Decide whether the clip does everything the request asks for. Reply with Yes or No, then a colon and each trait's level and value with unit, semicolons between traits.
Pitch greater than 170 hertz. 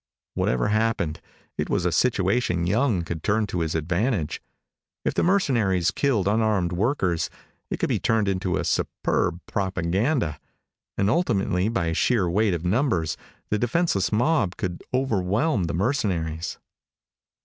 No: very low, 95 Hz